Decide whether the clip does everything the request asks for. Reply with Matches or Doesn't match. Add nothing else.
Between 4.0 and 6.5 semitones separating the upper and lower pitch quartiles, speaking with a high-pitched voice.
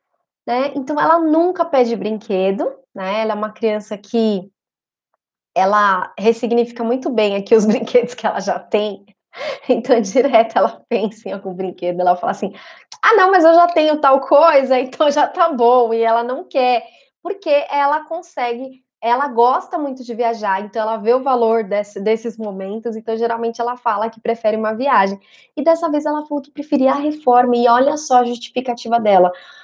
Matches